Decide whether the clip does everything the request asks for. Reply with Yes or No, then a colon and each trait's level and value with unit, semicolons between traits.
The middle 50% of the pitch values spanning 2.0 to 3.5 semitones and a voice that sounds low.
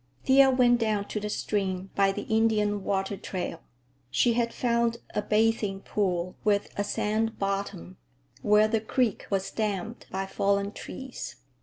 No: narrow, 2.5 semitones; high, 210 Hz